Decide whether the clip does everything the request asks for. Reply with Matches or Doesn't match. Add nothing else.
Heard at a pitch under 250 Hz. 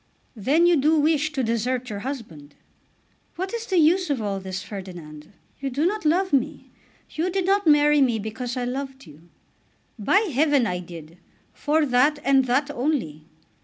Doesn't match